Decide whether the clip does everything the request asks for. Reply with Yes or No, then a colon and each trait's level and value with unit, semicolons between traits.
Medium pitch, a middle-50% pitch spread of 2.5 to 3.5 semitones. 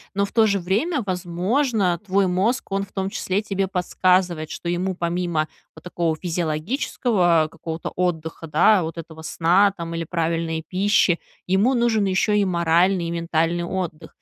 Yes: medium, 180 Hz; average, 2.9 semitones